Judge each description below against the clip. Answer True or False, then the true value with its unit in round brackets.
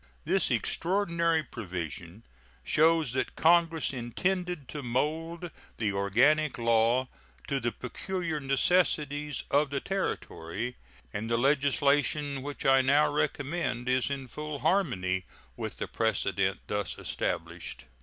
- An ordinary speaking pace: False (115 wpm)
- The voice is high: False (140 Hz)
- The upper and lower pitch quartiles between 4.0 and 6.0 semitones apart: True (5.1 semitones)